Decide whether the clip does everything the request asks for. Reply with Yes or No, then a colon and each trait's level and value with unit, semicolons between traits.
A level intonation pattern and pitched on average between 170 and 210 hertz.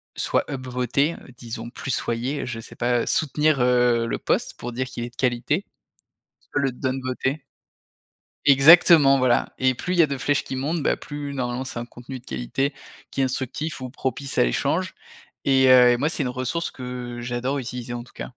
No: narrow, 2.3 semitones; low, 130 Hz